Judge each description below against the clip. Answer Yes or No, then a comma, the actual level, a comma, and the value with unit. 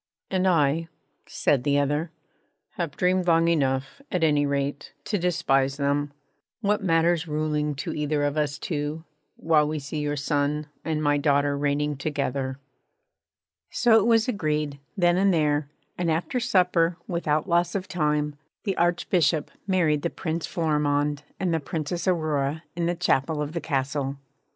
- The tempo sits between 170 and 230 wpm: No, average, 155 wpm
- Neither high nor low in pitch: Yes, medium, 155 Hz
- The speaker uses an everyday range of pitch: Yes, average, 3.1 semitones